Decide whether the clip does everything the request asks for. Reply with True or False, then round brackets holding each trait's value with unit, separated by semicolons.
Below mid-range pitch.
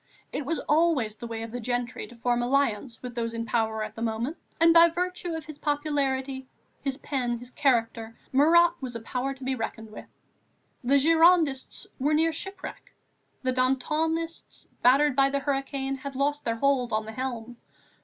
False (265 Hz)